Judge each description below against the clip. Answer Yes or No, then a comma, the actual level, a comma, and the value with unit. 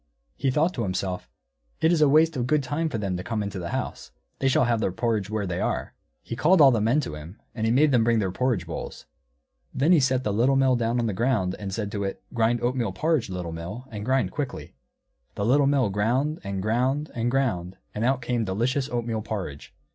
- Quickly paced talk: Yes, fast, 230 wpm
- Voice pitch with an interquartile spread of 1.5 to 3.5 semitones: No, average, 4.8 semitones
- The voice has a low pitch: Yes, low, 115 Hz